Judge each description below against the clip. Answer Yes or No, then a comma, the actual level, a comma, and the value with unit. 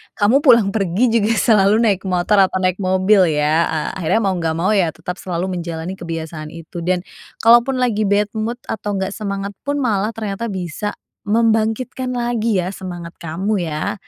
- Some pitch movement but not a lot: Yes, average, 4.0 semitones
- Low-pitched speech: No, high, 195 Hz